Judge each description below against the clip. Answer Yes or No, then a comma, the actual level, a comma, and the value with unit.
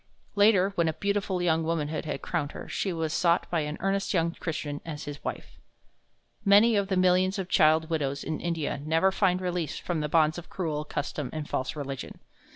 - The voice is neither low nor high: Yes, medium, 165 Hz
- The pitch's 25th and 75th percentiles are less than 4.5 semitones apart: Yes, average, 3.4 semitones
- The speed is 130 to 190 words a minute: No, average, 200 wpm